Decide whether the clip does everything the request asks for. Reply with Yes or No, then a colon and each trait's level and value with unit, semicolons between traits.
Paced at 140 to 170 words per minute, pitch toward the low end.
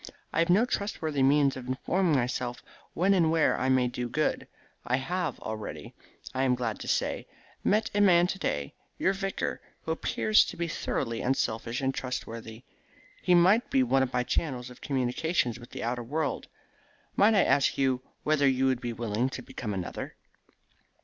No: average, 180 wpm; low, 130 Hz